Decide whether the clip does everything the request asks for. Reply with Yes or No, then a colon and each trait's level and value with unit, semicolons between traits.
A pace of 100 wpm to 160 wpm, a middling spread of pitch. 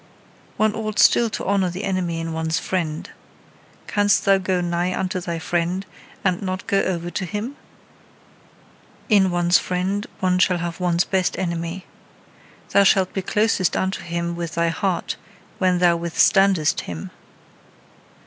No: average, 150 wpm; narrow, 2.2 semitones